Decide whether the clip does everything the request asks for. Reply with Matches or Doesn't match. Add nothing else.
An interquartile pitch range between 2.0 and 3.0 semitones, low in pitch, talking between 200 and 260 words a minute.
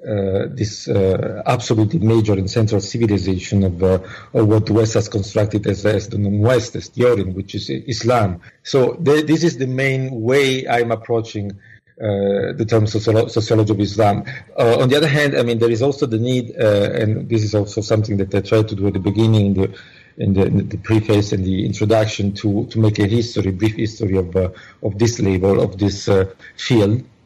Matches